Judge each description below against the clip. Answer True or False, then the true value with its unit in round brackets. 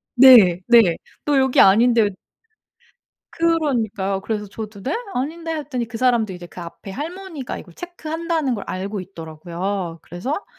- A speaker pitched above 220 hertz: True (230 Hz)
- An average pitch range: False (7.3 semitones)